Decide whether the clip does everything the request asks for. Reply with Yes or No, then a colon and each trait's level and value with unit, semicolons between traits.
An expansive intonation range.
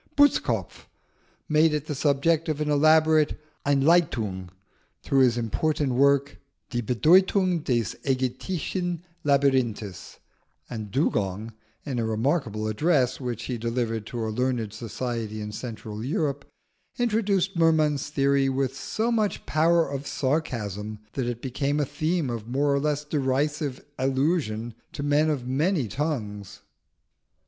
No: average, 4.6 semitones